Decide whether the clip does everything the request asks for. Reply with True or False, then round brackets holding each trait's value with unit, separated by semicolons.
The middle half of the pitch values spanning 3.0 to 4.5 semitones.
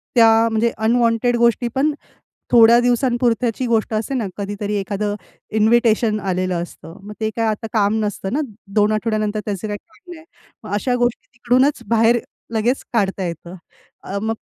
False (2.5 semitones)